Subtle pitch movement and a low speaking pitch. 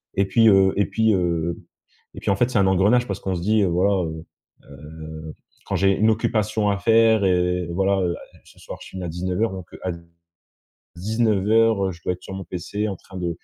No: average, 3.2 semitones; very low, 95 Hz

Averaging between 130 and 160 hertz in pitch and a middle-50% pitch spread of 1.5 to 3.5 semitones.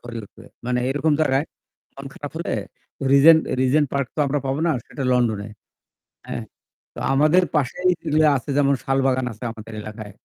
Yes: low, 135 Hz; average, 3.1 semitones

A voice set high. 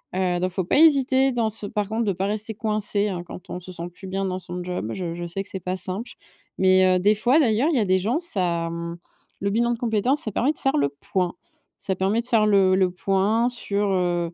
Yes: high, 195 Hz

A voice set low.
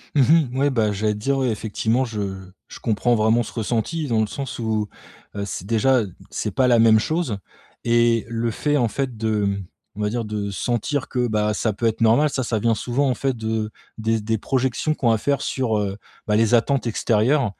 Yes: low, 115 Hz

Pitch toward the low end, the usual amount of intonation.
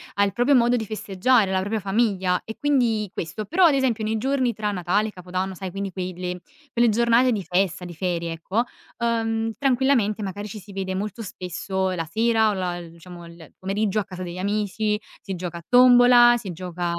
No: high, 200 Hz; average, 3.9 semitones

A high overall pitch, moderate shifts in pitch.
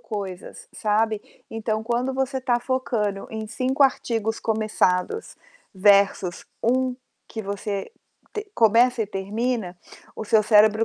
Yes: high, 220 Hz; average, 3.4 semitones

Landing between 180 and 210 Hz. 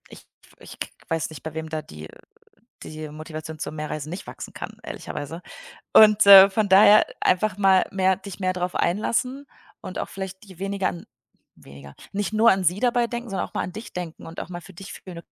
Yes: medium, 185 Hz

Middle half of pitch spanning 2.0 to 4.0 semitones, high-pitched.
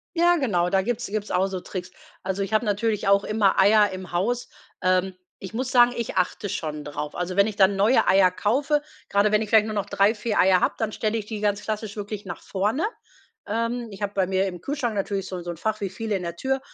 Yes: average, 2.7 semitones; high, 205 Hz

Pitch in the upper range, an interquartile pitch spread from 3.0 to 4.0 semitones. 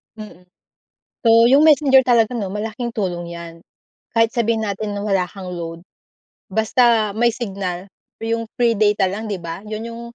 Yes: high, 215 Hz; average, 3.4 semitones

